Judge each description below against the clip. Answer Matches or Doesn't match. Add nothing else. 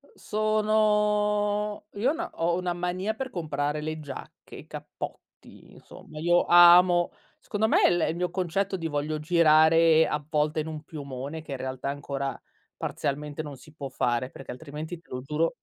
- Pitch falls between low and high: Matches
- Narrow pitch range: Doesn't match